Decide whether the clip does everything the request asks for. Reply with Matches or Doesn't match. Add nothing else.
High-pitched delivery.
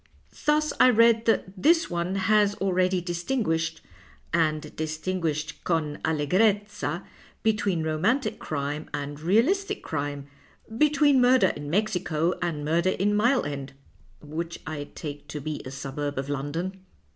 Doesn't match